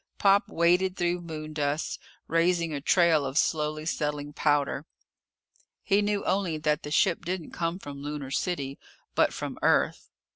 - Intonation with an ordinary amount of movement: Yes, average, 3.1 semitones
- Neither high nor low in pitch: Yes, medium, 160 Hz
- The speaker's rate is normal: Yes, average, 145 wpm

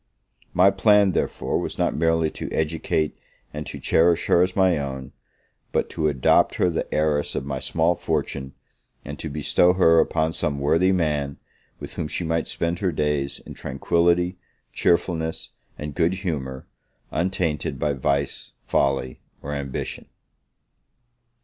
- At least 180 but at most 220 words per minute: No, average, 145 wpm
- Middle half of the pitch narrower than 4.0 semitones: Yes, average, 3.4 semitones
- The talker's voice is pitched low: Yes, very low, 80 Hz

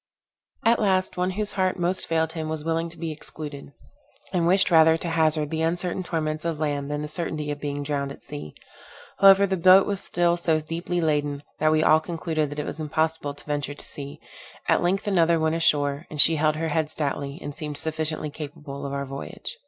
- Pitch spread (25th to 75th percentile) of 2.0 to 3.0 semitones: Yes, narrow, 2.5 semitones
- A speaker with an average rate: No, fast, 210 wpm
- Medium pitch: Yes, medium, 155 Hz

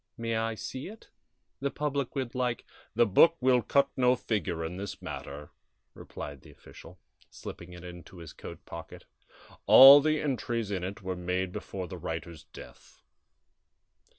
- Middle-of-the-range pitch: No, low, 110 Hz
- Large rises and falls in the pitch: Yes, wide, 6.5 semitones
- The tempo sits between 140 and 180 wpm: Yes, average, 160 wpm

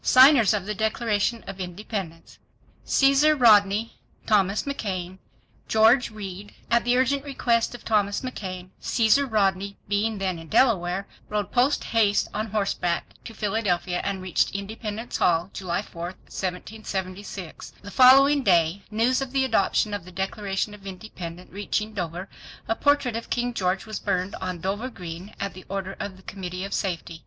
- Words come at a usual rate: Yes, average, 150 wpm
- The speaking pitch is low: No, high, 205 Hz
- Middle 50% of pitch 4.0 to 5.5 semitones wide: No, average, 3.5 semitones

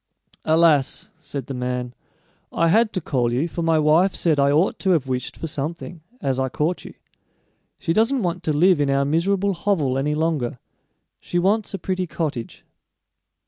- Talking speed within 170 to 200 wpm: Yes, average, 180 wpm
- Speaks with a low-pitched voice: No, medium, 160 Hz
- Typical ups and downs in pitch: Yes, average, 4.5 semitones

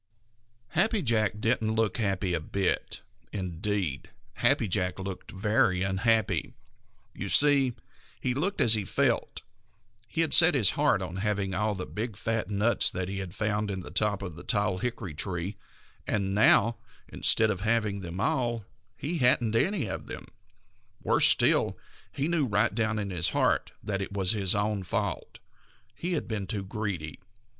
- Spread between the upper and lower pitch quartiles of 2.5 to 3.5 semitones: Yes, average, 3.1 semitones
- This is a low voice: Yes, low, 105 Hz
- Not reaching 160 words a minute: No, average, 170 wpm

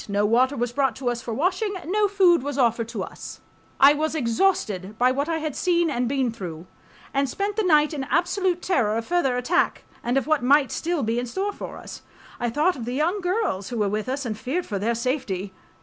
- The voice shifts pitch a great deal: Yes, wide, 6.7 semitones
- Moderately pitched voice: No, very high, 270 Hz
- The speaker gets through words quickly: Yes, fast, 230 wpm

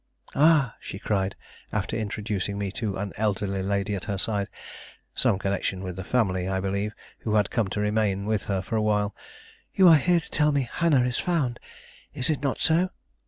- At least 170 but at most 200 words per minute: Yes, average, 195 wpm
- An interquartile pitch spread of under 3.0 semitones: No, average, 4.3 semitones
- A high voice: No, low, 105 Hz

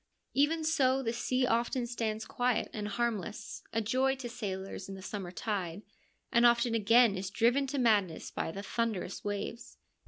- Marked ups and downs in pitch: No, average, 3.4 semitones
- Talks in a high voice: Yes, high, 230 Hz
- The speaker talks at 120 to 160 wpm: No, average, 175 wpm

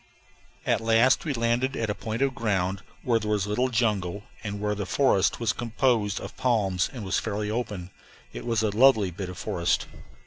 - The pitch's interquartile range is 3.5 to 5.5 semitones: No, average, 2.9 semitones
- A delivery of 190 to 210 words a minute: Yes, average, 195 wpm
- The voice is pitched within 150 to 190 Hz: No, low, 110 Hz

